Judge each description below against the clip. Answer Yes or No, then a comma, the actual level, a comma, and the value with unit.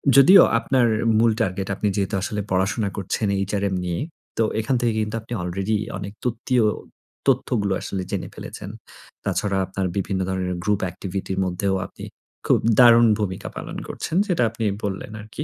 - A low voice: Yes, low, 105 Hz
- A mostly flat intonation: No, average, 3.3 semitones